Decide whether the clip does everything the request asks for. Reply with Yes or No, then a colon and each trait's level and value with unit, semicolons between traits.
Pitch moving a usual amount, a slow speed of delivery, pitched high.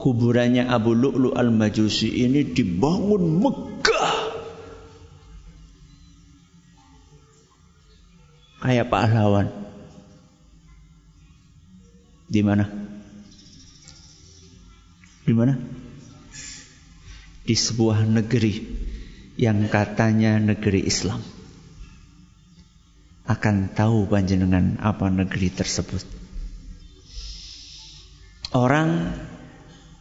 No: average, 4.2 semitones; slow, 60 wpm; low, 100 Hz